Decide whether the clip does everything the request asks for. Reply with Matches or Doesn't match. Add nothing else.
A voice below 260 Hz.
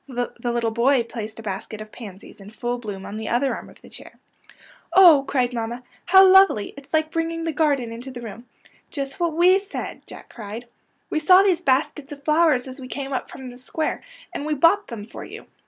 Doesn't match